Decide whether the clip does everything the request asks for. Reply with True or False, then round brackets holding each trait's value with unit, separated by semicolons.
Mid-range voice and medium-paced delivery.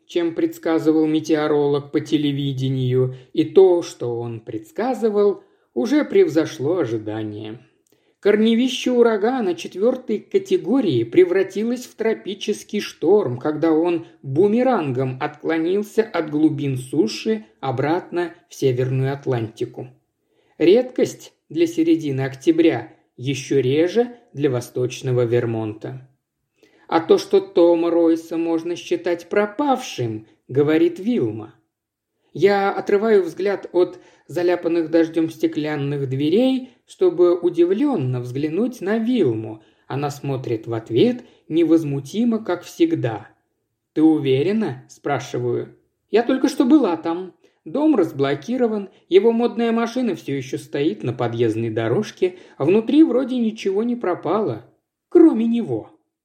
False (175 Hz; 105 wpm)